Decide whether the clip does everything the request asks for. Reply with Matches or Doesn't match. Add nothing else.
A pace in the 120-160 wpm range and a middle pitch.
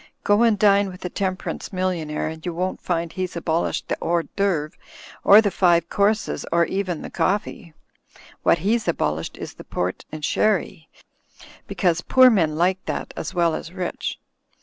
Doesn't match